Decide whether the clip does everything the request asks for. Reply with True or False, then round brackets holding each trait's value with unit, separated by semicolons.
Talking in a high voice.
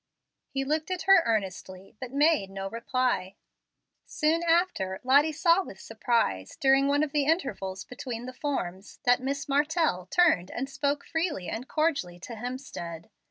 True (270 Hz)